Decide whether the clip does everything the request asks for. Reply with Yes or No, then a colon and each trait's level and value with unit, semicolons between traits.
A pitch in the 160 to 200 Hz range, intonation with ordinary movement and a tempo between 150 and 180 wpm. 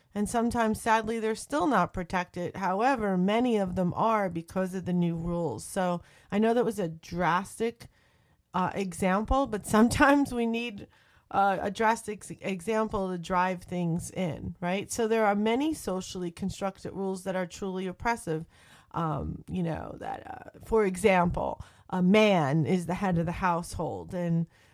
Yes: high, 190 Hz; average, 3.7 semitones; average, 160 wpm